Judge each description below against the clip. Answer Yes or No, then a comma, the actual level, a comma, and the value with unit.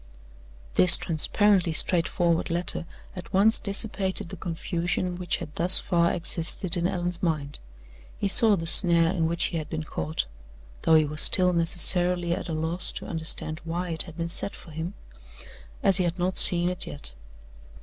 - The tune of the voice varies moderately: No, narrow, 1.8 semitones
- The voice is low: No, medium, 175 Hz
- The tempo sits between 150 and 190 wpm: Yes, average, 170 wpm